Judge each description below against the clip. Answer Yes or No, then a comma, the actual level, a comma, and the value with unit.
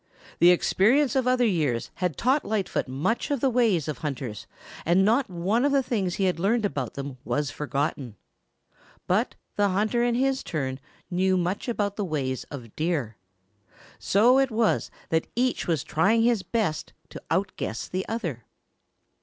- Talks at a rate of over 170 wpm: No, average, 165 wpm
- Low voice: No, high, 190 Hz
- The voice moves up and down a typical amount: No, wide, 7.6 semitones